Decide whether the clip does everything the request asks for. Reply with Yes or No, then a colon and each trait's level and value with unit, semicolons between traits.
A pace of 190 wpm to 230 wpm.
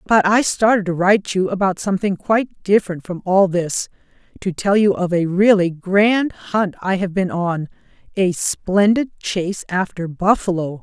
No: average, 155 wpm